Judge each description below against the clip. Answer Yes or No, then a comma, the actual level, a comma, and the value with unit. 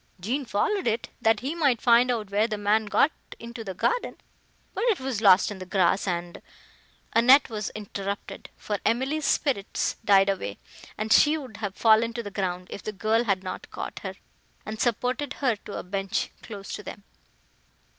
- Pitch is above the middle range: Yes, high, 215 Hz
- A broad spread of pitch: No, average, 3.7 semitones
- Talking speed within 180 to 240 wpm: Yes, average, 185 wpm